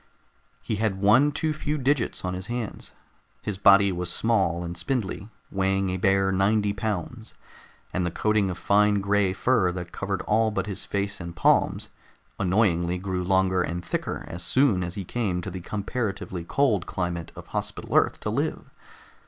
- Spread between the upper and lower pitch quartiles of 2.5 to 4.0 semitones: Yes, average, 3.0 semitones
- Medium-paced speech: Yes, average, 170 wpm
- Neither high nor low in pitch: No, very low, 95 Hz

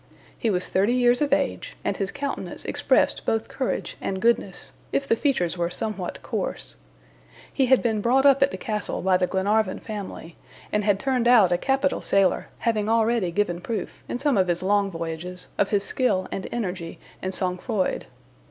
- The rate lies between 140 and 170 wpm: No, average, 185 wpm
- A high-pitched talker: Yes, high, 210 Hz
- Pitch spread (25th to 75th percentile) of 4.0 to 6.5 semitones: Yes, average, 4.7 semitones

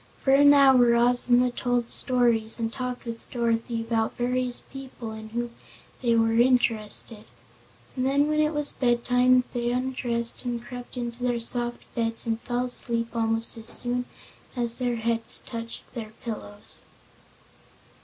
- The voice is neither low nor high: No, high, 240 Hz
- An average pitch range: No, narrow, 1.5 semitones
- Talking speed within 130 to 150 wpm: Yes, average, 145 wpm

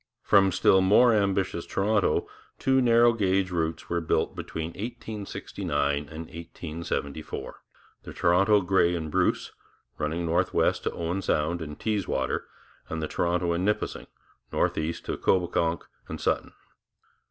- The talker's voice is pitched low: Yes, very low, 85 Hz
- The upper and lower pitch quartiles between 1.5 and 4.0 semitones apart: Yes, average, 3.4 semitones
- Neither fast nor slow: No, slow, 130 wpm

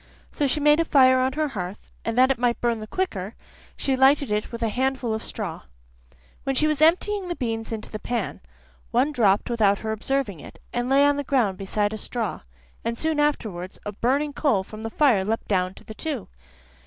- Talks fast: Yes, fast, 215 wpm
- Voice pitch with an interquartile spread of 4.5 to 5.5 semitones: Yes, average, 4.8 semitones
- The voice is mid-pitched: No, high, 240 Hz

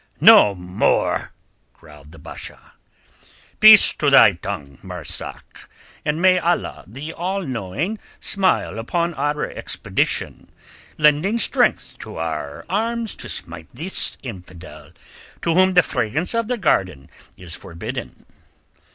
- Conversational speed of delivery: No, slow, 120 wpm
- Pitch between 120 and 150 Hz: Yes, medium, 140 Hz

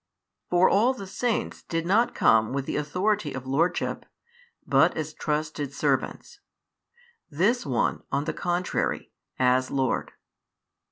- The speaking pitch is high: No, medium, 155 Hz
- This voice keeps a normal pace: No, slow, 125 wpm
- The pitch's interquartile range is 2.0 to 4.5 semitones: No, wide, 5.4 semitones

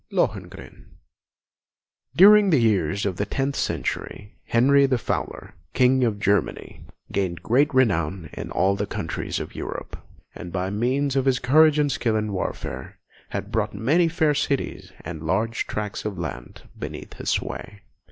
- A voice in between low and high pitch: No, low, 115 Hz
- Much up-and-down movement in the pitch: Yes, wide, 6.0 semitones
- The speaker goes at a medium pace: Yes, average, 155 wpm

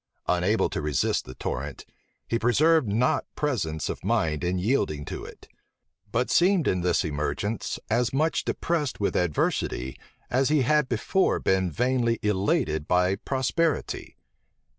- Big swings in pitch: Yes, wide, 7.4 semitones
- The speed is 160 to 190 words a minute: No, average, 140 wpm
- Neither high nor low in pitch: No, low, 115 Hz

